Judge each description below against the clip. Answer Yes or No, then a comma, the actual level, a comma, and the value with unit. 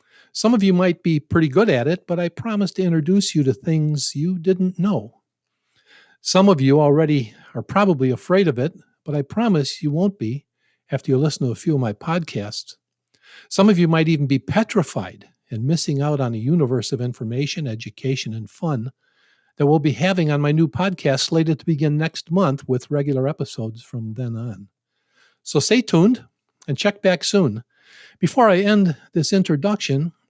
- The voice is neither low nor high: Yes, medium, 155 Hz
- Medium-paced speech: Yes, average, 185 wpm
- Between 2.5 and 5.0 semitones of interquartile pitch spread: No, wide, 5.6 semitones